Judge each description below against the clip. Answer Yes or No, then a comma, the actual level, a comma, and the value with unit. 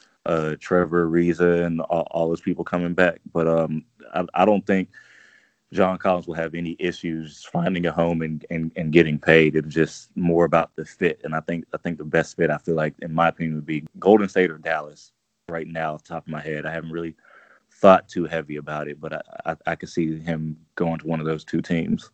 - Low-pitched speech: Yes, very low, 80 Hz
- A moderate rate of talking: No, fast, 235 wpm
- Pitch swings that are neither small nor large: No, narrow, 1.4 semitones